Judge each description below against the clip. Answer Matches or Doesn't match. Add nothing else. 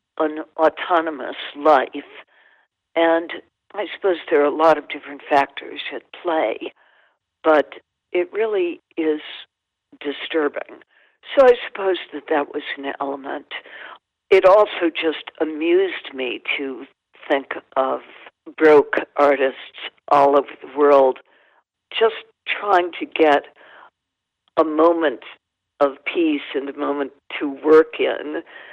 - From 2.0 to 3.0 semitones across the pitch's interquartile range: Doesn't match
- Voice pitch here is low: Doesn't match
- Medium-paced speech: Doesn't match